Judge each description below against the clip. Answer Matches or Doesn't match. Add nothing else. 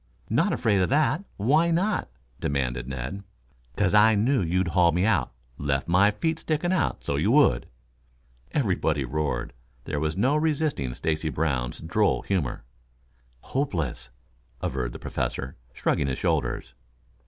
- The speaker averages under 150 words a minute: Matches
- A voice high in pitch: Doesn't match